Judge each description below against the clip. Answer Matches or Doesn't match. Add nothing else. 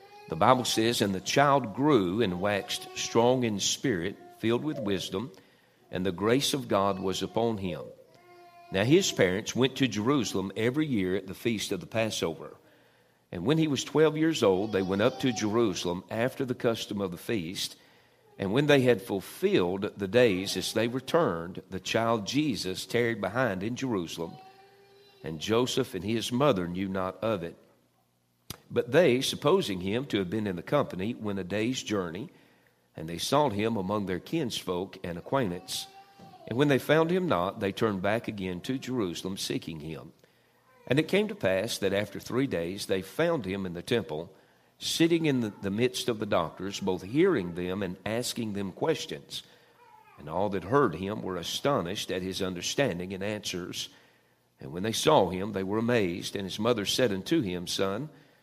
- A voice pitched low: Matches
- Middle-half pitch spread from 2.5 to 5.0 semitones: Doesn't match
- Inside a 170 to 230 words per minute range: Matches